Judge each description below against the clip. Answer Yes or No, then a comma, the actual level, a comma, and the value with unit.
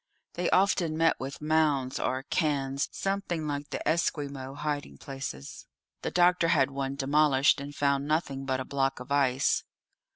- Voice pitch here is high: No, medium, 140 Hz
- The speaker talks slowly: No, average, 155 wpm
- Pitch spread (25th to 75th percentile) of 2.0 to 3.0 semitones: Yes, narrow, 2.6 semitones